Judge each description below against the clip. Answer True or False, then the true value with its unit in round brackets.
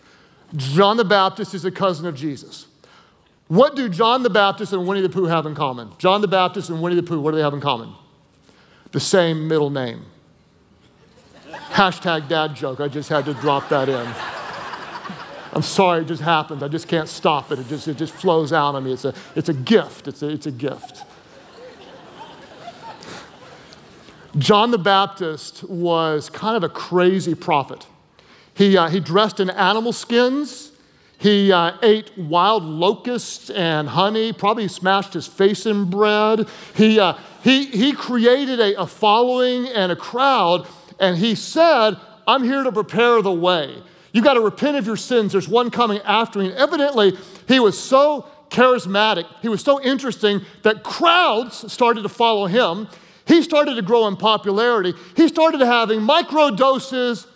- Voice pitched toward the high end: True (195 Hz)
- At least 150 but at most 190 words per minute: True (170 wpm)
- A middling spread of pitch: False (5.7 semitones)